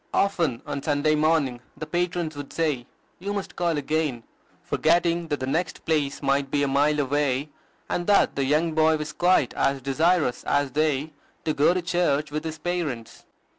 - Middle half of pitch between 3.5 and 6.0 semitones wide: No, average, 3.0 semitones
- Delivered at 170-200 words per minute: Yes, average, 175 wpm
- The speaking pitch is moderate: Yes, medium, 155 Hz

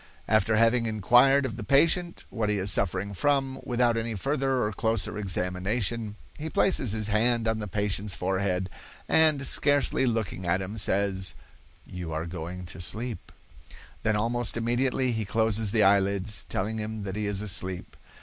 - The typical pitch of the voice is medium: No, low, 110 Hz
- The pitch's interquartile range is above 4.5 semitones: No, average, 3.7 semitones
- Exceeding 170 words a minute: No, average, 160 wpm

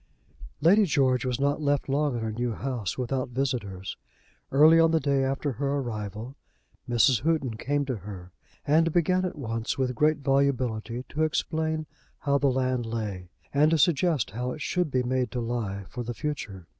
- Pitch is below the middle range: Yes, low, 130 Hz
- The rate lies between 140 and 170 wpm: No, average, 180 wpm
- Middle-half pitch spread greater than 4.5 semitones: No, average, 4.1 semitones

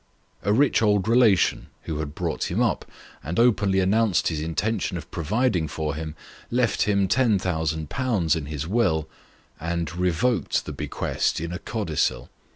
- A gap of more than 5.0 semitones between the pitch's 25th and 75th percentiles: Yes, wide, 5.6 semitones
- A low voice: Yes, very low, 90 Hz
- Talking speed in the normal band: Yes, average, 150 wpm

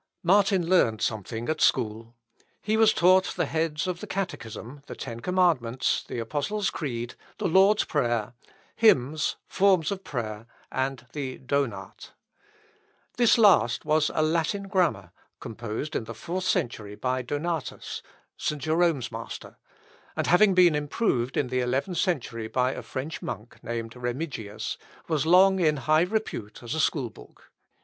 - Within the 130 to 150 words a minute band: Yes, average, 145 wpm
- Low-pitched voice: No, medium, 145 Hz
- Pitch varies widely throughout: Yes, wide, 7.0 semitones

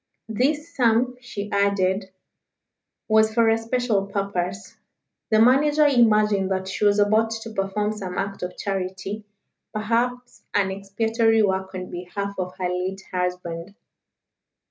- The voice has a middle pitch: No, high, 205 Hz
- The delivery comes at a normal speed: No, slow, 130 wpm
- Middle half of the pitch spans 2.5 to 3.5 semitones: Yes, average, 2.9 semitones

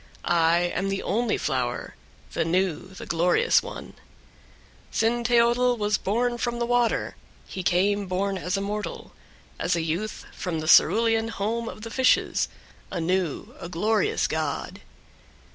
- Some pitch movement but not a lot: Yes, average, 4.7 semitones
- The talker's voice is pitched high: Yes, high, 200 Hz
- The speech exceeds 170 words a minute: No, average, 145 wpm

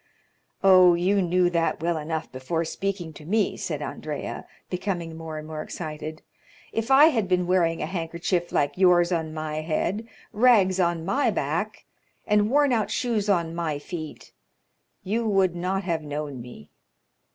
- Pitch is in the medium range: Yes, medium, 175 Hz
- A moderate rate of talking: Yes, average, 160 wpm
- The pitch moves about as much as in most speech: Yes, average, 3.6 semitones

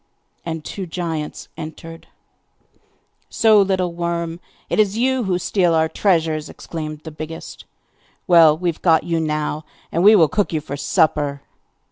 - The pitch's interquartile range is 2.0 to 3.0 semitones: Yes, average, 2.7 semitones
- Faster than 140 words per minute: Yes, average, 150 wpm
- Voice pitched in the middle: Yes, medium, 165 Hz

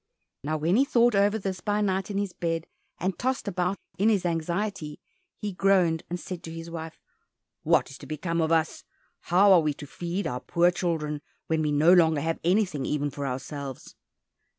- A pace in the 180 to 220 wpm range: Yes, average, 195 wpm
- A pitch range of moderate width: Yes, average, 3.7 semitones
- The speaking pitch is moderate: Yes, medium, 170 Hz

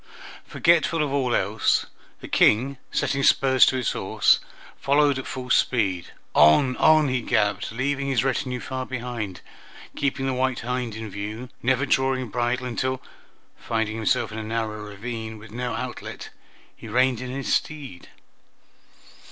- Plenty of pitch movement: No, average, 3.0 semitones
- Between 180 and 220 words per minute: No, average, 150 wpm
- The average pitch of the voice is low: Yes, low, 125 Hz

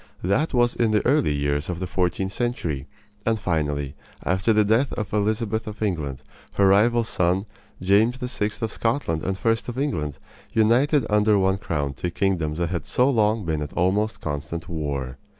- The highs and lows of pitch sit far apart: Yes, wide, 5.7 semitones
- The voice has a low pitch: Yes, low, 100 Hz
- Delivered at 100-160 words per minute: No, average, 175 wpm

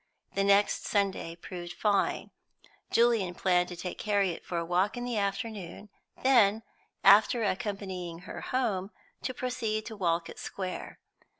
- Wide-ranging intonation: No, average, 3.3 semitones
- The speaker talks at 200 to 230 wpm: No, slow, 135 wpm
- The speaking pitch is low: No, high, 200 Hz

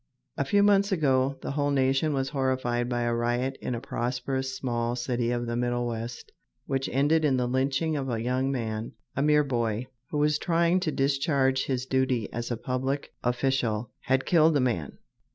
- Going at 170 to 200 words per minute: Yes, average, 190 wpm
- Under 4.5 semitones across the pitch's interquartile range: Yes, narrow, 2.5 semitones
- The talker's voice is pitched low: Yes, low, 130 Hz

